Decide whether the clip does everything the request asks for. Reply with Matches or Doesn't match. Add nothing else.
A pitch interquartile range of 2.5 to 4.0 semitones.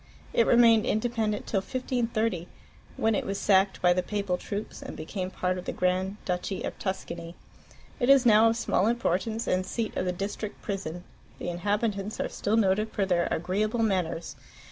Matches